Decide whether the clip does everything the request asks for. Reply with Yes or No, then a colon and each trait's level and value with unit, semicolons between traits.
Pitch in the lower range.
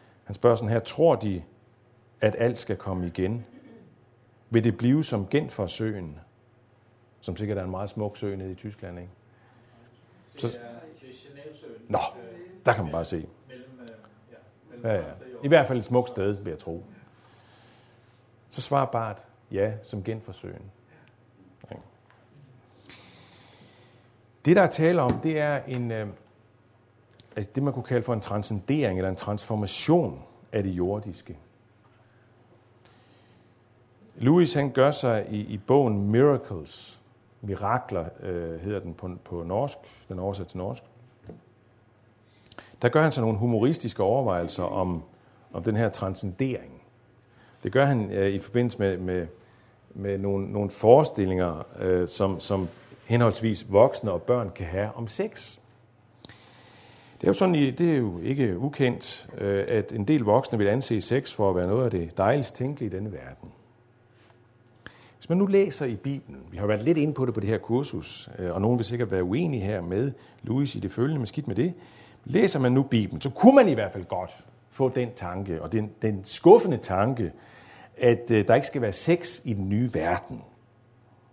Yes: low, 120 Hz